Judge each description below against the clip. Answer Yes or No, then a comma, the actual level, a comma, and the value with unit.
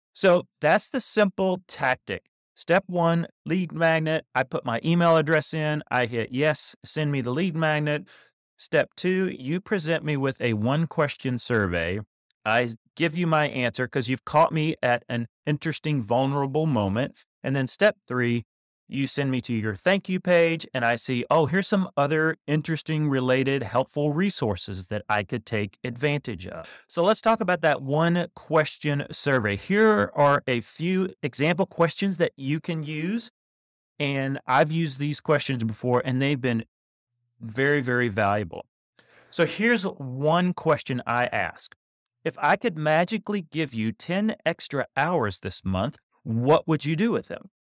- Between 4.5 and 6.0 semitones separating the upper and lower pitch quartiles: Yes, average, 5.2 semitones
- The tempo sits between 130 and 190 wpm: Yes, average, 160 wpm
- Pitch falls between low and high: Yes, medium, 150 Hz